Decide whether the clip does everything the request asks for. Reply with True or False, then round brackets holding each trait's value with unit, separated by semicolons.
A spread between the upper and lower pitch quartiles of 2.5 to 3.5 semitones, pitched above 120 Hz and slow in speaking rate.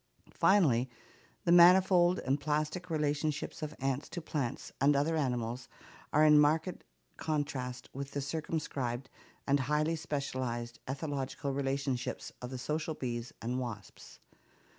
True (3.2 semitones; 140 Hz; 125 wpm)